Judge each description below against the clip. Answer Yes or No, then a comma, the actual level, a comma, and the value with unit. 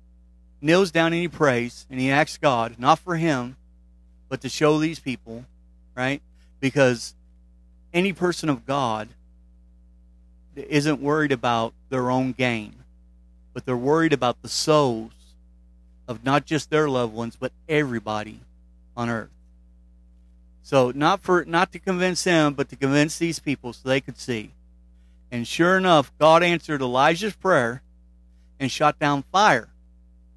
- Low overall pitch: Yes, low, 125 Hz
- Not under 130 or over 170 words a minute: Yes, average, 140 wpm